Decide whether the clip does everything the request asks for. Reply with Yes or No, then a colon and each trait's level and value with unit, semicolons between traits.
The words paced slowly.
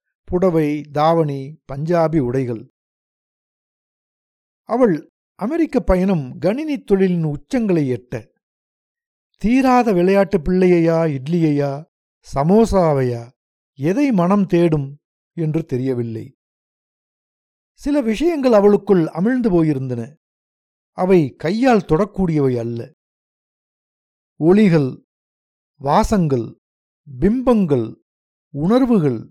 Yes: slow, 70 wpm